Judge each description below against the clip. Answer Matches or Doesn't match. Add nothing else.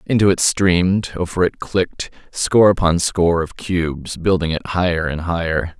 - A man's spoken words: Matches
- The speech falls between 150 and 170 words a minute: Matches